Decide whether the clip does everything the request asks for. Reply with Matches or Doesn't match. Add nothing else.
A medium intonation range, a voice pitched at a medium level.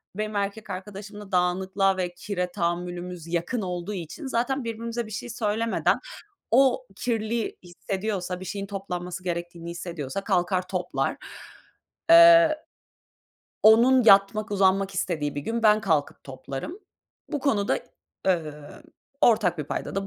Doesn't match